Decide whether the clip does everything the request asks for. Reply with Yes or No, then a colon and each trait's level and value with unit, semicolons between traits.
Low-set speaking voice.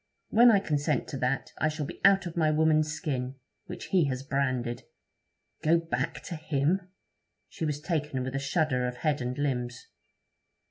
No: medium, 150 Hz